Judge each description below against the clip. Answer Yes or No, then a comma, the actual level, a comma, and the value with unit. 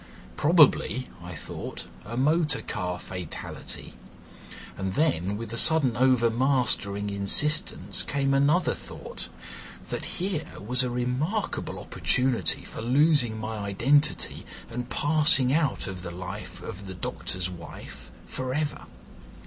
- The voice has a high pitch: No, low, 125 Hz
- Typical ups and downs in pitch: No, wide, 6.6 semitones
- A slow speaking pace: Yes, slow, 120 wpm